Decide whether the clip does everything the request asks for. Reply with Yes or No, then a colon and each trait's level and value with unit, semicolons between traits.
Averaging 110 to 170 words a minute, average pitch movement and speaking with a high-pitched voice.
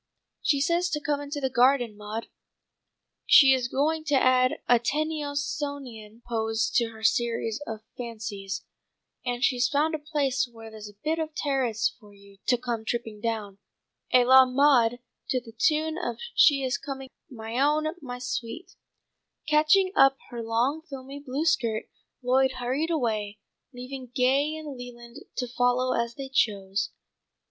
Yes: average, 155 wpm; average, 3.8 semitones; very high, 255 Hz